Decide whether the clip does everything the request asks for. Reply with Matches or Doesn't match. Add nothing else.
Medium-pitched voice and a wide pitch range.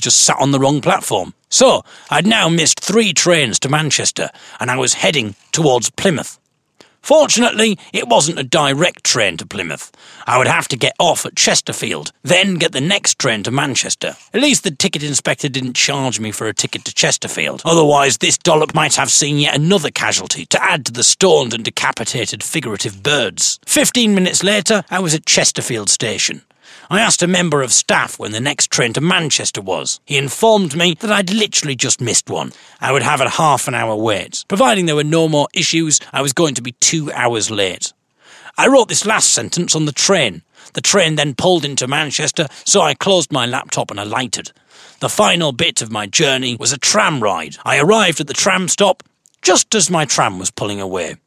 Matches